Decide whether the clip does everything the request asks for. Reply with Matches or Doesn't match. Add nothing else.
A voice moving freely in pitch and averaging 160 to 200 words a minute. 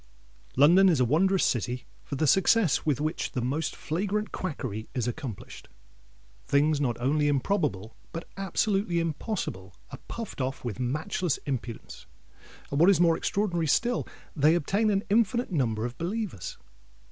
Doesn't match